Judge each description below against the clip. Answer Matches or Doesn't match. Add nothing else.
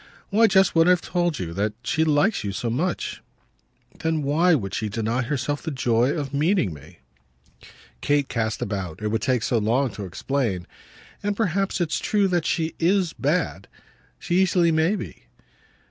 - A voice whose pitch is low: Doesn't match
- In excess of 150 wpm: Matches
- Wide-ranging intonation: Matches